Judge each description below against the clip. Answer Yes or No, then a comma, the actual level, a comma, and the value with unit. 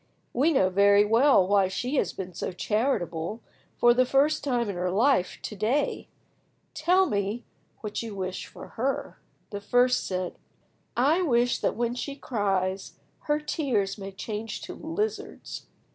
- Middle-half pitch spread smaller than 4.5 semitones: No, wide, 5.6 semitones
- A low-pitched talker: No, high, 225 Hz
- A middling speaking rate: Yes, average, 160 wpm